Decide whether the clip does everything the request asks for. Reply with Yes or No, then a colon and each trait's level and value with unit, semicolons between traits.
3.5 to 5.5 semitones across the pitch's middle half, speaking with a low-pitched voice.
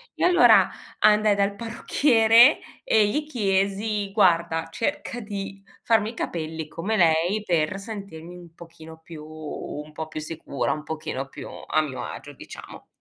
No: average, 5.1 semitones; high, 190 Hz